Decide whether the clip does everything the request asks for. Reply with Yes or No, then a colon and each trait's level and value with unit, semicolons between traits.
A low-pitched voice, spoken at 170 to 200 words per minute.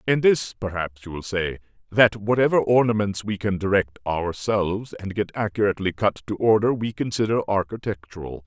No: low, 105 Hz; average, 155 wpm